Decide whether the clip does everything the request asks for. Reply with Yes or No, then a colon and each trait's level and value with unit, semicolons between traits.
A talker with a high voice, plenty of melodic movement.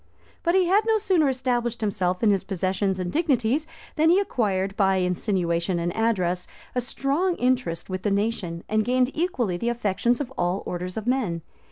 Yes: high, 220 Hz; wide, 5.8 semitones